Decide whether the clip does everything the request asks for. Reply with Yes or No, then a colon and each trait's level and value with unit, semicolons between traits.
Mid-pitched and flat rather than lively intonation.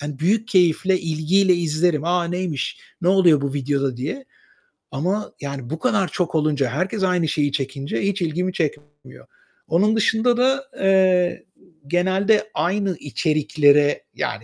No: medium, 175 Hz; average, 4.6 semitones